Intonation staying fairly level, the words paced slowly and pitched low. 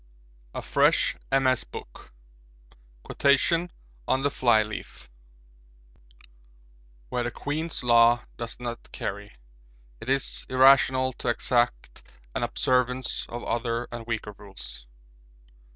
Yes: narrow, 2.0 semitones; slow, 105 wpm; low, 120 Hz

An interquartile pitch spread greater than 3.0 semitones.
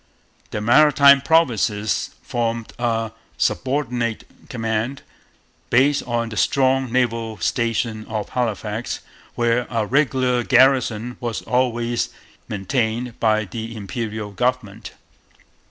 No: narrow, 2.4 semitones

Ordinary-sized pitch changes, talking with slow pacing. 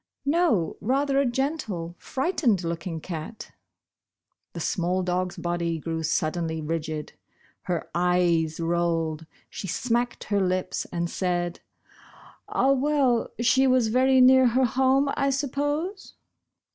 No: wide, 7.6 semitones; slow, 120 wpm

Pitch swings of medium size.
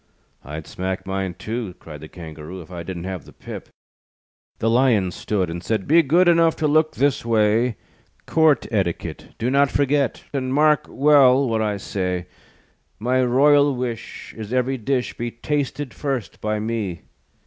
No: wide, 6.6 semitones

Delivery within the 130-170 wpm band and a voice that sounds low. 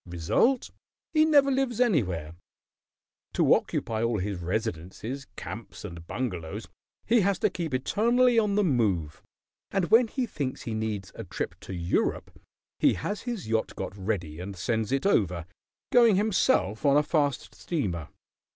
Yes: average, 150 wpm; low, 125 Hz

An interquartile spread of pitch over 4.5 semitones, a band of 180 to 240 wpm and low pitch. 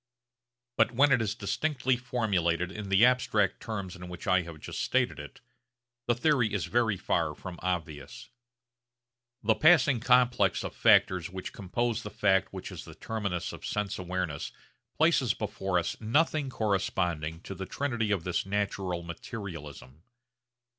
No: average, 5.2 semitones; average, 150 wpm; low, 100 Hz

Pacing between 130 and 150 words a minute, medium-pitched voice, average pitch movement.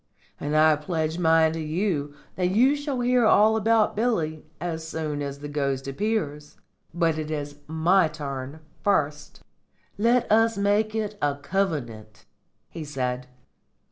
No: average, 140 wpm; medium, 160 Hz; wide, 6.1 semitones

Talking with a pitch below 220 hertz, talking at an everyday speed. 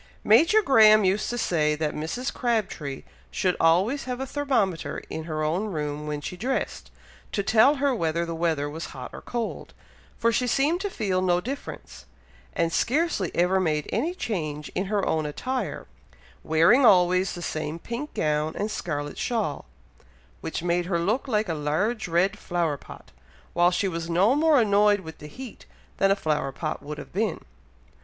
Yes: medium, 185 Hz; average, 175 wpm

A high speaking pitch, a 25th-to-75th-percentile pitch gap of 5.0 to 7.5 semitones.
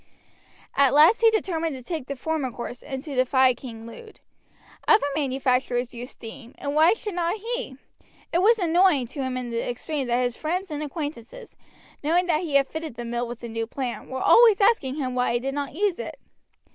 Yes: very high, 280 Hz; wide, 5.5 semitones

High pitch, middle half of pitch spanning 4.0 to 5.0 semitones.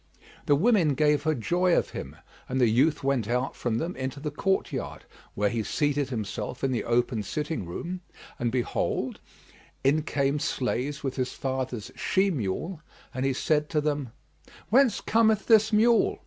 No: medium, 140 Hz; average, 4.6 semitones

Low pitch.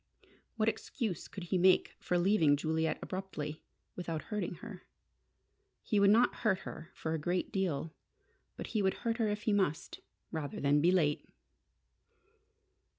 No: medium, 185 Hz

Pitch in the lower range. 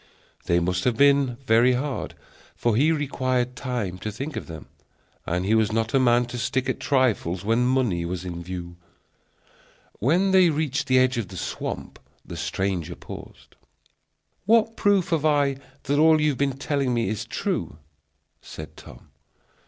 Yes: low, 125 Hz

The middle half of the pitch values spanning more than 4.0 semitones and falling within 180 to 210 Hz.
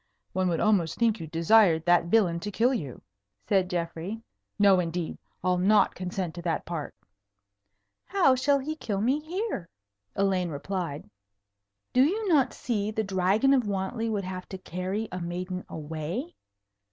Yes: average, 4.5 semitones; high, 190 Hz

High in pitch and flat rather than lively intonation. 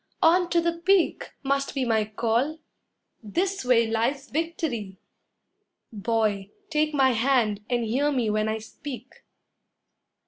No: very high, 255 Hz; wide, 5.5 semitones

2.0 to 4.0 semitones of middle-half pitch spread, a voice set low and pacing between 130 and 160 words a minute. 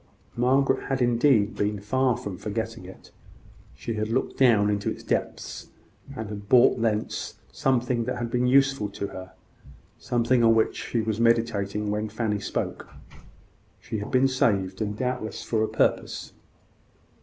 Yes: average, 3.1 semitones; low, 115 Hz; average, 155 wpm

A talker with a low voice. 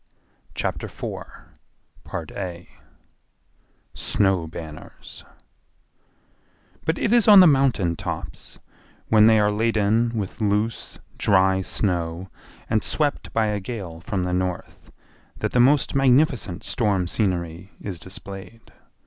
Yes: low, 105 Hz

